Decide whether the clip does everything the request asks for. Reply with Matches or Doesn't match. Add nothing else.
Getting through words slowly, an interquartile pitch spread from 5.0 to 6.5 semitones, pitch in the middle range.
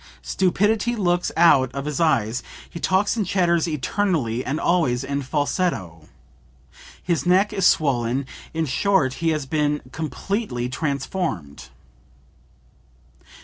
Matches